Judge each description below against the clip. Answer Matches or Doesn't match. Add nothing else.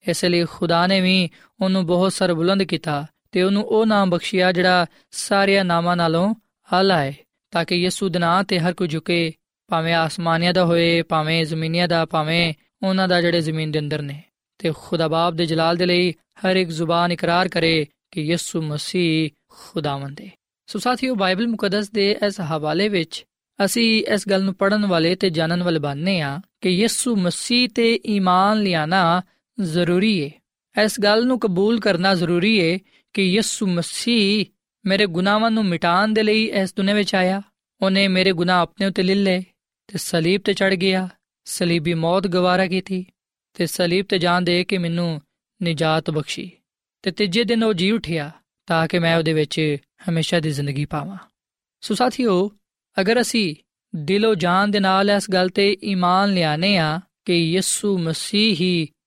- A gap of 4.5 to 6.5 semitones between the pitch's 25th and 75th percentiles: Doesn't match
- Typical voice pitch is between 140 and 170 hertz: Doesn't match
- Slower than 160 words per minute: Doesn't match